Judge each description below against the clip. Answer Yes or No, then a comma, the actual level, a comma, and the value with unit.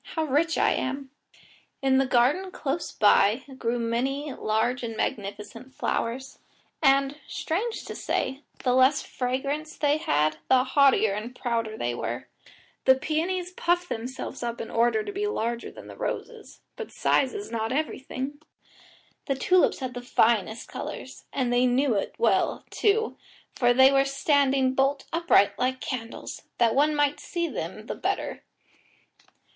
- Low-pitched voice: No, very high, 265 Hz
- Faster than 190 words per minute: No, average, 150 wpm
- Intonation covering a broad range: No, average, 3.8 semitones